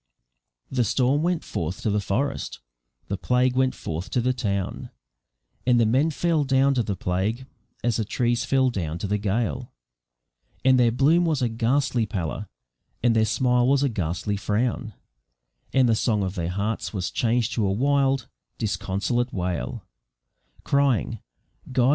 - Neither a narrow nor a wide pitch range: Yes, average, 4.3 semitones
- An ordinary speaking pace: Yes, average, 160 wpm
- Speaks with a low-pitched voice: Yes, low, 120 Hz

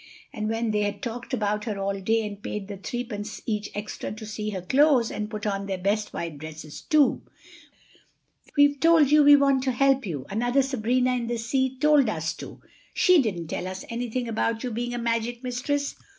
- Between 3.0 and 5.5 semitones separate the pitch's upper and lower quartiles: Yes, average, 3.8 semitones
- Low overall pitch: No, high, 225 Hz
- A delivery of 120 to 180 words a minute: No, average, 195 wpm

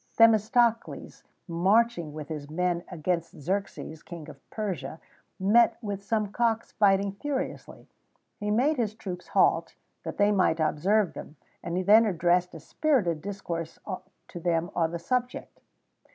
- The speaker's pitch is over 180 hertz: Yes, high, 190 Hz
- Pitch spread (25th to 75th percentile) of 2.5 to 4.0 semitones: No, average, 4.4 semitones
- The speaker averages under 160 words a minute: Yes, average, 150 wpm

